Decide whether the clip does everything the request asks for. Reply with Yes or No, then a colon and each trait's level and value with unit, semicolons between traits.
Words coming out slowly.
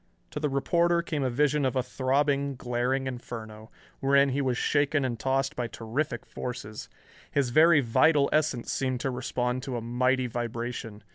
No: average, 165 wpm